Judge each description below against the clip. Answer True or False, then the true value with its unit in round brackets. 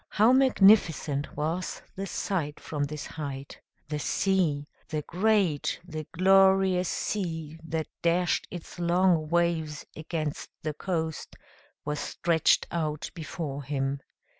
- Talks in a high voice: False (160 Hz)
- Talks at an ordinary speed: False (115 wpm)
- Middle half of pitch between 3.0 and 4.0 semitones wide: True (3.5 semitones)